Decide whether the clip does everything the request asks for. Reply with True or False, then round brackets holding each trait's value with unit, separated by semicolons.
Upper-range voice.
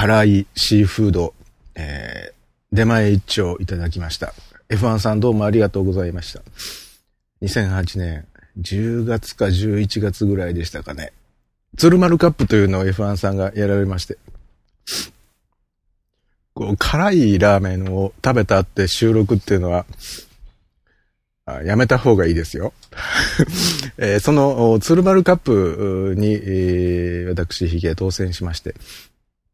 False (100 Hz)